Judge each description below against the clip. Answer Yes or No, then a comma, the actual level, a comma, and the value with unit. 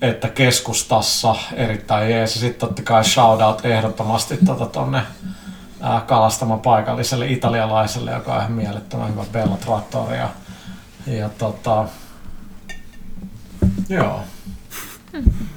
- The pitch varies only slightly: Yes, narrow, 2.3 semitones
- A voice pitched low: Yes, low, 115 Hz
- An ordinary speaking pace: No, slow, 90 wpm